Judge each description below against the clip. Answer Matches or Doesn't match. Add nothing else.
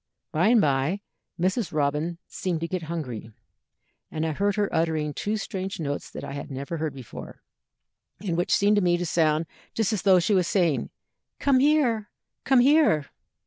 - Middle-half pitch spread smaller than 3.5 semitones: Doesn't match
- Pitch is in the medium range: Matches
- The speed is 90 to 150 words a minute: Doesn't match